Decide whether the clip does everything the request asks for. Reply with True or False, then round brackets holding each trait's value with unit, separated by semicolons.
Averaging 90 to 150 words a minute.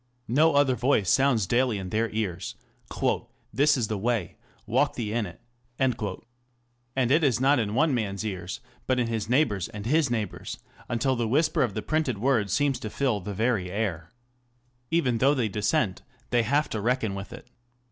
False (185 wpm)